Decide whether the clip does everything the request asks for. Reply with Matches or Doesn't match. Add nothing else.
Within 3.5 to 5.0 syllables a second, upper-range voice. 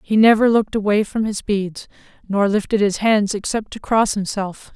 Matches